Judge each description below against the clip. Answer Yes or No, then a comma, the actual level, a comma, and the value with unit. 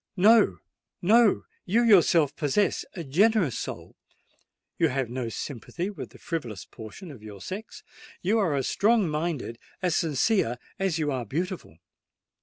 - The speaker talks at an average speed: No, slow, 130 wpm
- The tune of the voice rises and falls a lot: Yes, wide, 7.2 semitones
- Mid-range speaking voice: Yes, medium, 165 Hz